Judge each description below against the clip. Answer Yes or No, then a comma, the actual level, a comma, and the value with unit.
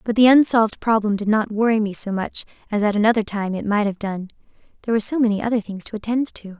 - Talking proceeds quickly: Yes, fast, 245 wpm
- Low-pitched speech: No, high, 215 Hz